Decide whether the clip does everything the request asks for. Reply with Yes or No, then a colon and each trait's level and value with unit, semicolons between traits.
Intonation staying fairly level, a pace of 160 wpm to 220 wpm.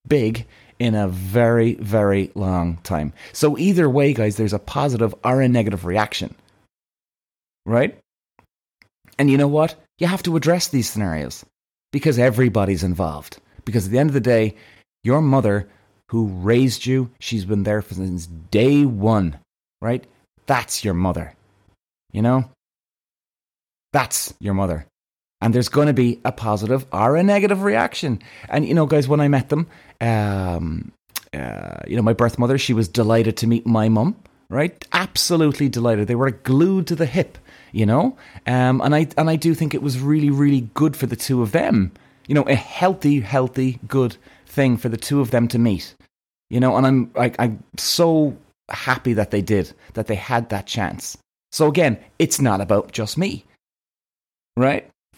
No: average, 5.1 semitones; average, 170 wpm